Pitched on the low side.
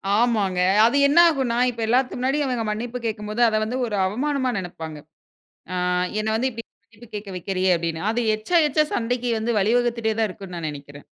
No: high, 225 Hz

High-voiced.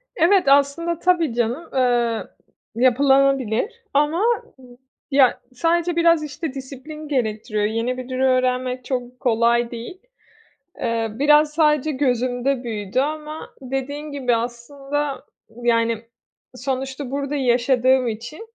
Yes: very high, 265 Hz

